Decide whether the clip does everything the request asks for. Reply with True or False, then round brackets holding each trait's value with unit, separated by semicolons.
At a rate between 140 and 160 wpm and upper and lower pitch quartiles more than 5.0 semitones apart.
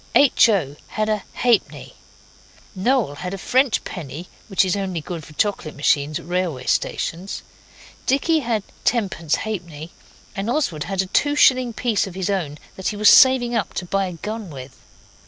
False (175 wpm; 5.4 semitones)